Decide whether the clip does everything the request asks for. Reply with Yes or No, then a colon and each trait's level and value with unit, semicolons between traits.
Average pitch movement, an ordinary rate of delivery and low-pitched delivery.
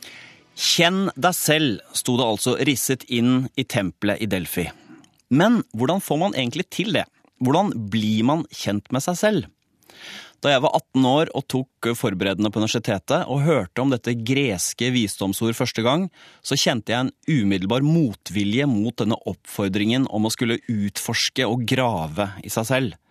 Yes: average, 4.0 semitones; average, 160 wpm; low, 125 Hz